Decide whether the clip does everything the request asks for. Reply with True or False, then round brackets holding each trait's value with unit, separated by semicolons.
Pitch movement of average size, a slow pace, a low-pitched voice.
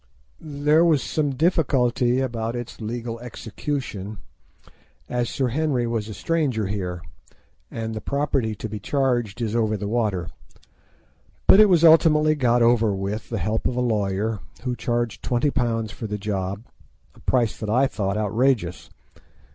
False (3.8 semitones; 145 wpm; 120 Hz)